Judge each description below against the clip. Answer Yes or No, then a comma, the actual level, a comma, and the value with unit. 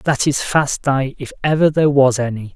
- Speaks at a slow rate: No, fast, 210 wpm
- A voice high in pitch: No, low, 135 Hz